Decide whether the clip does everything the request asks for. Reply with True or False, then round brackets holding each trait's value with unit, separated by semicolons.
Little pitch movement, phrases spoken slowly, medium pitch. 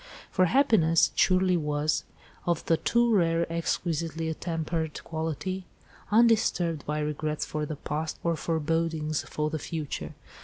True (2.1 semitones; 130 wpm; 165 Hz)